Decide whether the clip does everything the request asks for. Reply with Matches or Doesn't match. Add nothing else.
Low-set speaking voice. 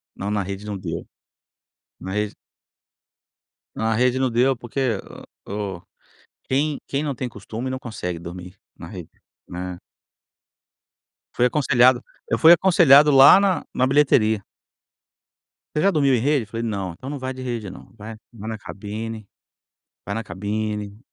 Matches